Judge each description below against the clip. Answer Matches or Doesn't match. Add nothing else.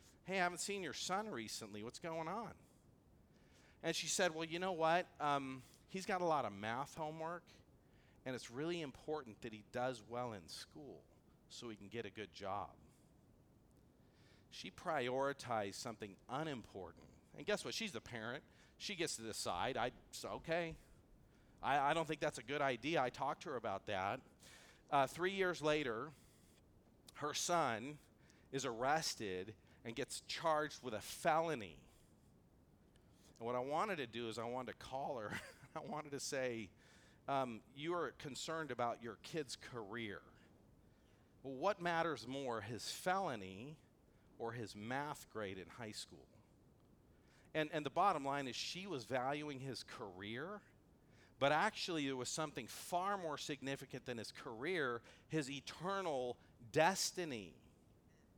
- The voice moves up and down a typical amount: Doesn't match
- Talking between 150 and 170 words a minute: Matches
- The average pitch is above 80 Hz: Matches